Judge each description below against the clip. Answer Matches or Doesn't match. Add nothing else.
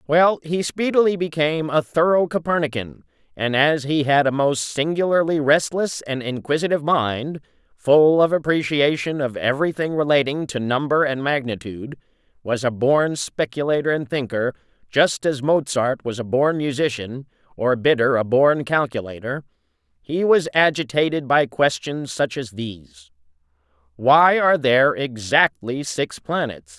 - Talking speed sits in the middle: Doesn't match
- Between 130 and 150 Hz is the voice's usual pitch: Matches